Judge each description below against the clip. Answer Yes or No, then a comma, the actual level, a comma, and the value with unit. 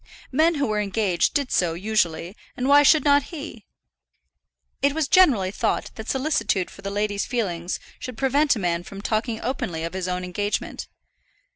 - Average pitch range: No, wide, 7.1 semitones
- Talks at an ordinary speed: Yes, average, 170 wpm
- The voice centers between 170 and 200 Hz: No, high, 215 Hz